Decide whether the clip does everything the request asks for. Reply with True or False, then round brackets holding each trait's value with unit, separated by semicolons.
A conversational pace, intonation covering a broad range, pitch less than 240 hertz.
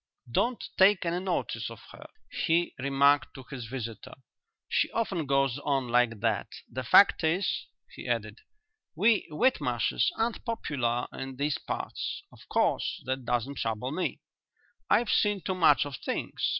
True (150 wpm; 6.7 semitones; 140 Hz)